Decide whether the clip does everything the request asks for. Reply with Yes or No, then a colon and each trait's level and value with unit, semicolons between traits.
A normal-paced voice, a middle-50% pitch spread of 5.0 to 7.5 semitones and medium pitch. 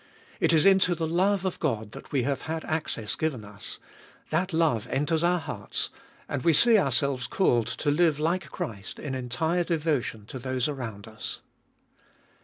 Yes: average, 170 wpm; wide, 5.5 semitones; medium, 150 Hz